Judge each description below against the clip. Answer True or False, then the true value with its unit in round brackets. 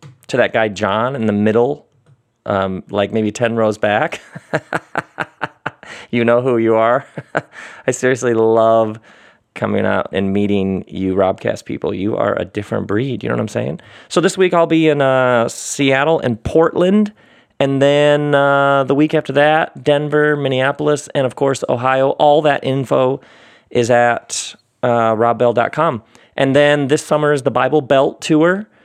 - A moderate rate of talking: True (160 wpm)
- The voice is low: True (130 Hz)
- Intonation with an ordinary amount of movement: True (4.2 semitones)